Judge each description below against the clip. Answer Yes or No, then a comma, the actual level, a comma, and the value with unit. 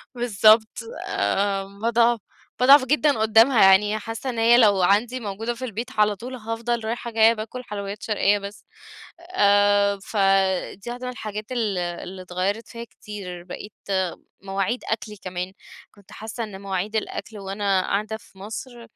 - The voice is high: Yes, high, 215 Hz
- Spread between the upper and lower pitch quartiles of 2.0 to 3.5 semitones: Yes, average, 2.8 semitones